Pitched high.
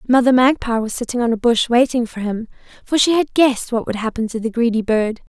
Yes: high, 240 Hz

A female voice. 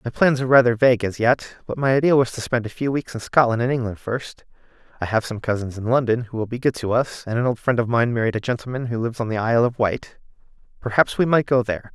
No: male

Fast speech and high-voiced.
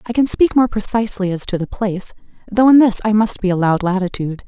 Yes: fast, 230 wpm; high, 205 Hz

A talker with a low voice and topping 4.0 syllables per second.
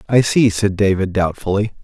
Yes: low, 100 Hz; 5.0 syllables/s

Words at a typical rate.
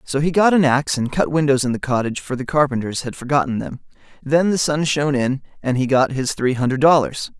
No: fast, 235 wpm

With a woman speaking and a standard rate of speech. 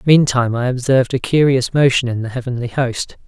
No: male; average, 185 wpm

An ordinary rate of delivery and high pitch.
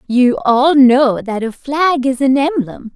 Yes: average, 185 wpm; very high, 265 Hz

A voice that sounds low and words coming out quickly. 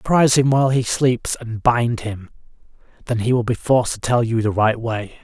Yes: low, 120 Hz; fast, 220 wpm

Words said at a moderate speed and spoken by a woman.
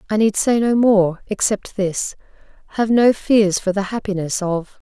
Yes: average, 170 wpm; female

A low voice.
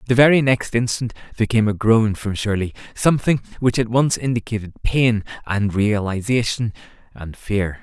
Yes: low, 110 Hz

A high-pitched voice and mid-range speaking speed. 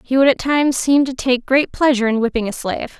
No: very high, 260 Hz; fast, 260 wpm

